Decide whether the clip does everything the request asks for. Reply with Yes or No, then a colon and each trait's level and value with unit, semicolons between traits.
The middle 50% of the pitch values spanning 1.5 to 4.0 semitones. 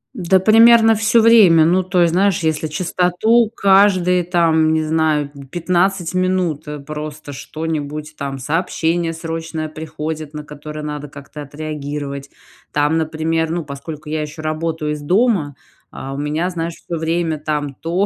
Yes: average, 2.8 semitones